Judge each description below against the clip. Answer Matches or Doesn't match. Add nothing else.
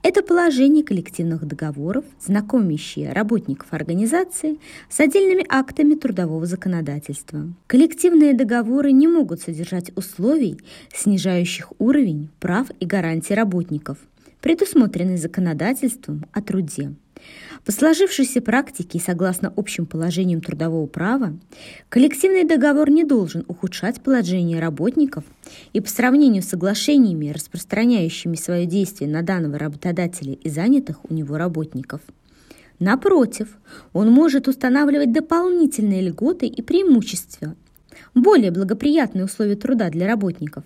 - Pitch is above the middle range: Matches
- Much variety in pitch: Matches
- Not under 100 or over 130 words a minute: Matches